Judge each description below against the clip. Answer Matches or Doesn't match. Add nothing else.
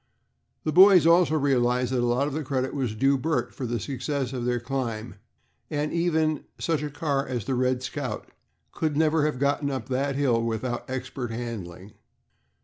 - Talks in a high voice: Doesn't match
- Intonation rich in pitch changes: Doesn't match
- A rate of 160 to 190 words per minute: Matches